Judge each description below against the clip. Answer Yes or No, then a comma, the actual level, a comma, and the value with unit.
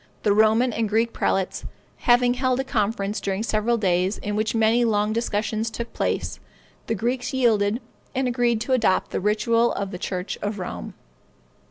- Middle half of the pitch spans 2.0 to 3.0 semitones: Yes, narrow, 2.5 semitones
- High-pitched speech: Yes, high, 220 Hz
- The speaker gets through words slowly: No, average, 170 wpm